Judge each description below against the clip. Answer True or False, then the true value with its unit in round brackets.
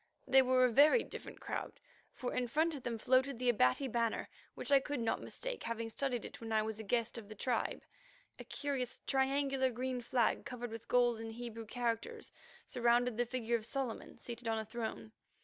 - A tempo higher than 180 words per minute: True (195 wpm)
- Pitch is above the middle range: True (245 Hz)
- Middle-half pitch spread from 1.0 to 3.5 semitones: True (2.5 semitones)